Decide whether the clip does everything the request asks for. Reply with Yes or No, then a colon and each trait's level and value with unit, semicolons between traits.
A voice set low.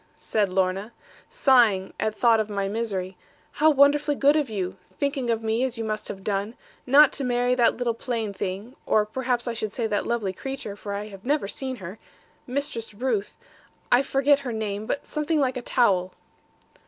No: high, 230 Hz